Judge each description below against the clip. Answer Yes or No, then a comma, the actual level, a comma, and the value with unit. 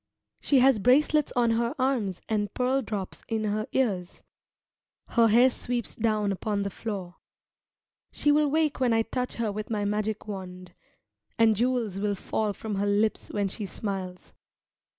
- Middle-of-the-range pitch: No, high, 220 Hz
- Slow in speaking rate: No, average, 160 wpm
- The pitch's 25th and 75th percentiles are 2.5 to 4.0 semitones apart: Yes, average, 3.5 semitones